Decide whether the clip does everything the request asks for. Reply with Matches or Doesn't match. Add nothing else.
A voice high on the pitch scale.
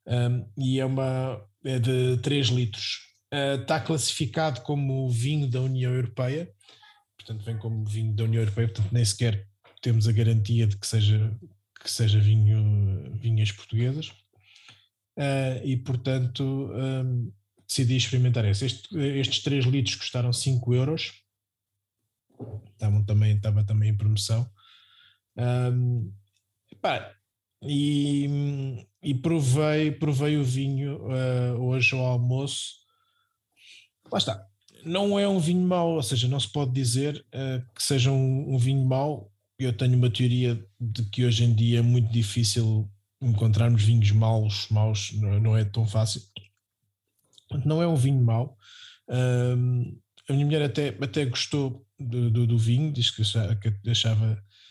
Doesn't match